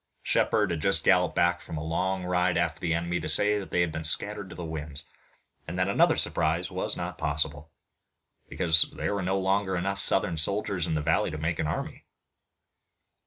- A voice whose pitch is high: No, very low, 85 Hz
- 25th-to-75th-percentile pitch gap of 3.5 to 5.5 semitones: No, average, 3.0 semitones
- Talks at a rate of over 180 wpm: Yes, average, 200 wpm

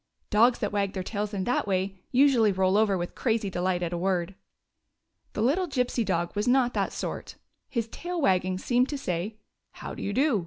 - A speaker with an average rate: No, fast, 210 wpm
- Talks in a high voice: Yes, high, 205 Hz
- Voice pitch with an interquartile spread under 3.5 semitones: No, average, 4.7 semitones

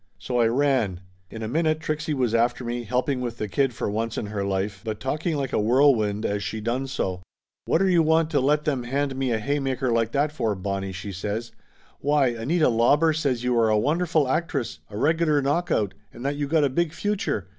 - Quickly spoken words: Yes, fast, 215 wpm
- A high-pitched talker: No, low, 130 Hz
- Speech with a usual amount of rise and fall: Yes, average, 5.0 semitones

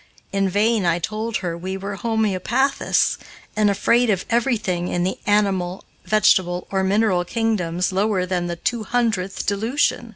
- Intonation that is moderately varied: Yes, average, 3.5 semitones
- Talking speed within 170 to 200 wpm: No, average, 150 wpm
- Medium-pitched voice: No, high, 200 Hz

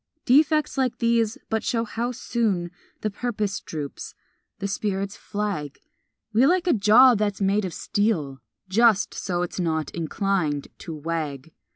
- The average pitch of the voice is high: Yes, high, 205 Hz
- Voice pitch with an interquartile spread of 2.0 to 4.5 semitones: No, wide, 5.4 semitones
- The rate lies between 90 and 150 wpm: Yes, average, 145 wpm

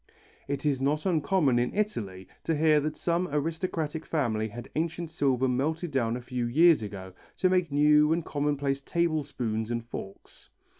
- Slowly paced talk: No, average, 165 wpm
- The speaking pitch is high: No, medium, 145 Hz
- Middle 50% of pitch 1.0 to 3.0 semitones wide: No, average, 4.8 semitones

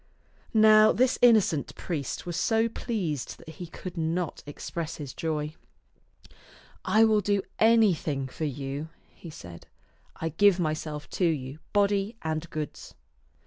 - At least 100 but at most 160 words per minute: Yes, average, 145 wpm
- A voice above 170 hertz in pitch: No, medium, 165 Hz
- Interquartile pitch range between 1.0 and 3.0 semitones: No, average, 5.3 semitones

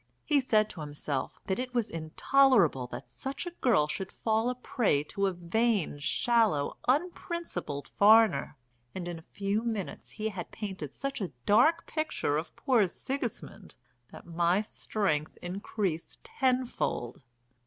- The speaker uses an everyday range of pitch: No, wide, 6.8 semitones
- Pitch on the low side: No, high, 205 Hz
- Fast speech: No, average, 145 wpm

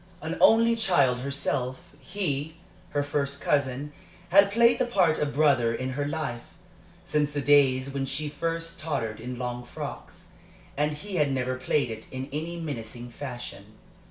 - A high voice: No, medium, 140 Hz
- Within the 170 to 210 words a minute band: No, average, 155 wpm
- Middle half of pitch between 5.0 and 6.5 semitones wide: No, average, 3.6 semitones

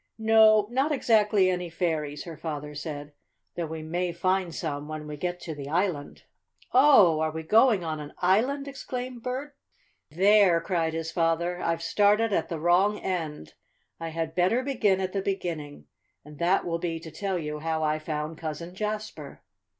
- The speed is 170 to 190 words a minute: Yes, average, 175 wpm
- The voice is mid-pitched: Yes, medium, 175 Hz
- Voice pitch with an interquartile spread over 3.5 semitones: Yes, average, 4.6 semitones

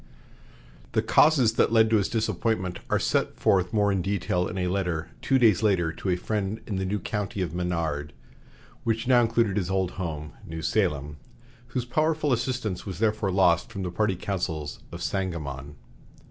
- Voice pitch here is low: Yes, very low, 95 Hz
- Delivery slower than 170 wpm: No, average, 180 wpm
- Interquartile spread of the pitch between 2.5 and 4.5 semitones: Yes, average, 4.2 semitones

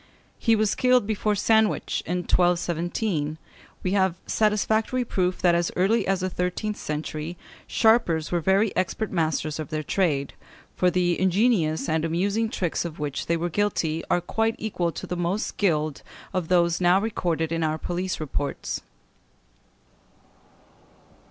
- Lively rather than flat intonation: No, average, 4.1 semitones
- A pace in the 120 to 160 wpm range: Yes, average, 145 wpm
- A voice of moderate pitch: Yes, medium, 180 Hz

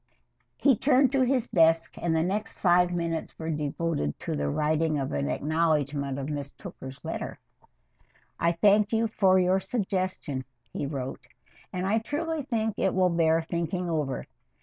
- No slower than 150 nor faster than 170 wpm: Yes, average, 160 wpm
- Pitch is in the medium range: Yes, medium, 170 Hz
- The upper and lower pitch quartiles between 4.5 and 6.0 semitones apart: Yes, average, 5.1 semitones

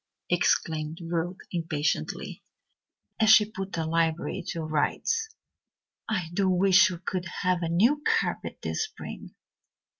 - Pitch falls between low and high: Yes, medium, 180 Hz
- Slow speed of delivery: Yes, slow, 125 wpm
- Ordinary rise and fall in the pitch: Yes, average, 3.8 semitones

